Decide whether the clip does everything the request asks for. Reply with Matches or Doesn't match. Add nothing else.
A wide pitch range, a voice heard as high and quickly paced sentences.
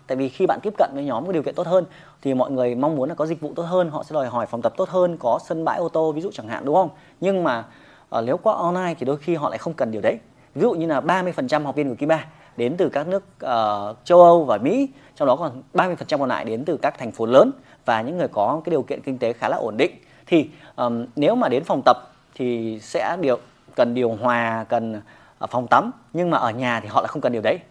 Doesn't match